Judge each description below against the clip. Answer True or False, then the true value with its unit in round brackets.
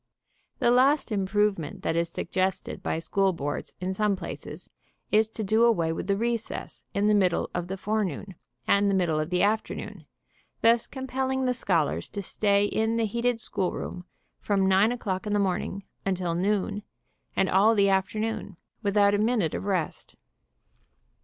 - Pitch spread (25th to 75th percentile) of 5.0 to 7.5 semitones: False (2.8 semitones)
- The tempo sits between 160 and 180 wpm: True (170 wpm)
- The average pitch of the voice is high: True (200 Hz)